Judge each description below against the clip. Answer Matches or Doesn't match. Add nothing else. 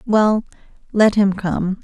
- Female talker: Matches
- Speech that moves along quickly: Doesn't match